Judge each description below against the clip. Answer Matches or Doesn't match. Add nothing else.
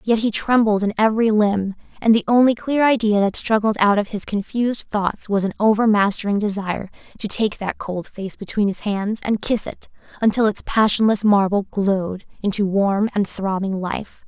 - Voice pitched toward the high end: Matches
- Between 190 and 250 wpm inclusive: Doesn't match